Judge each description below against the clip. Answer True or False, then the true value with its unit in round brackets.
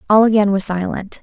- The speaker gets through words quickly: False (195 wpm)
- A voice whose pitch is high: True (205 Hz)